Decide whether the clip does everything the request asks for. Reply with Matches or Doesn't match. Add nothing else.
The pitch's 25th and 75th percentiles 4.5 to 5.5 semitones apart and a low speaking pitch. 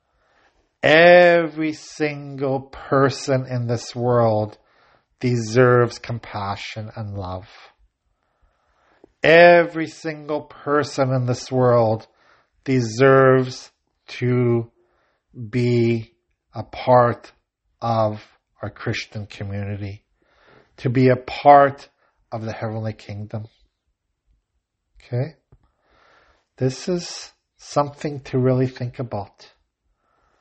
Doesn't match